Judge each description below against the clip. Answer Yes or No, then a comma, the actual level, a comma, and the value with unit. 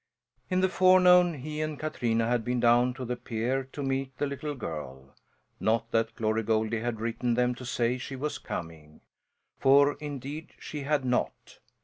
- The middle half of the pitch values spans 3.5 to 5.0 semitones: Yes, average, 4.2 semitones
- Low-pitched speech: Yes, low, 125 Hz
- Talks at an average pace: Yes, average, 170 wpm